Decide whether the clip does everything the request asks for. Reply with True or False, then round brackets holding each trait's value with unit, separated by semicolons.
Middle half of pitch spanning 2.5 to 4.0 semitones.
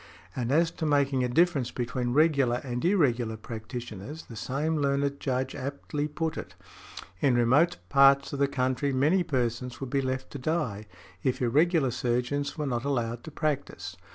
True (3.2 semitones)